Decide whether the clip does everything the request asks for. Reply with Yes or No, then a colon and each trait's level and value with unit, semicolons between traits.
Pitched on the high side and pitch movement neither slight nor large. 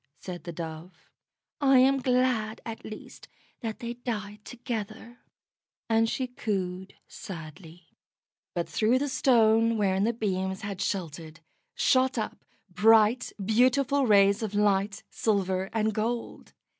Yes: high, 215 Hz; average, 3.9 semitones